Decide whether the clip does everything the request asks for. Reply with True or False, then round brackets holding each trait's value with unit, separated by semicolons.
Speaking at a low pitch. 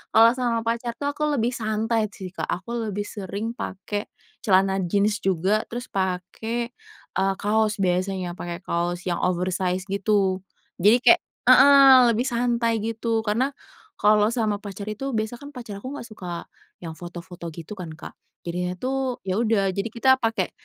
False (210 Hz)